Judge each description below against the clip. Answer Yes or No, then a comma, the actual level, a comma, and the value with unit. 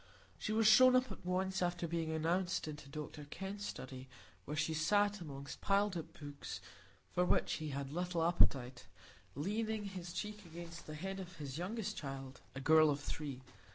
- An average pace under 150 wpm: No, average, 175 wpm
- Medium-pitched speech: Yes, medium, 170 Hz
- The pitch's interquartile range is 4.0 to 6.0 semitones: Yes, average, 4.6 semitones